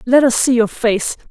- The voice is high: Yes, high, 240 Hz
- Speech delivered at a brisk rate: Yes, fast, 230 wpm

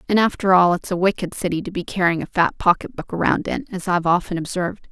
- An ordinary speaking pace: No, fast, 230 wpm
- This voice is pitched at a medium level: Yes, medium, 180 Hz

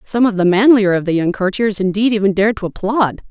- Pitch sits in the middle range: No, high, 205 Hz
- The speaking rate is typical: No, fast, 235 wpm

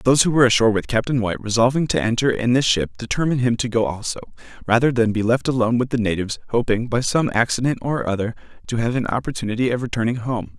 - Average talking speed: No, fast, 220 wpm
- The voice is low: Yes, low, 120 Hz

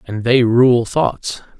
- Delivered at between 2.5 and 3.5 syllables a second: Yes, 3.0 syllables/s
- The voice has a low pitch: Yes, low, 120 Hz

